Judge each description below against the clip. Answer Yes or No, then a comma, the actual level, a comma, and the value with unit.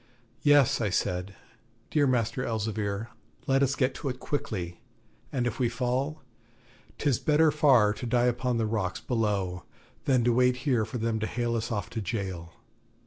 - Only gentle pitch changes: No, average, 3.4 semitones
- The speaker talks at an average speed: Yes, average, 170 wpm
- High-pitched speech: No, low, 120 Hz